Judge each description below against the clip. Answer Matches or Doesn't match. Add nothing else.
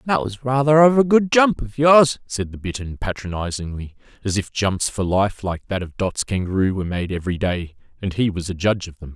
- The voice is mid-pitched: Doesn't match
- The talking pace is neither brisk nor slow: Doesn't match